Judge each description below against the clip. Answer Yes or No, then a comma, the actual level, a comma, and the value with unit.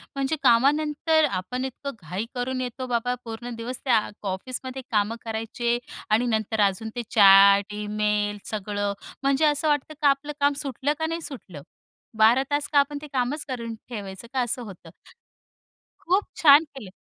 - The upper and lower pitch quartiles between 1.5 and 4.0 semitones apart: No, average, 4.9 semitones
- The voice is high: Yes, high, 245 Hz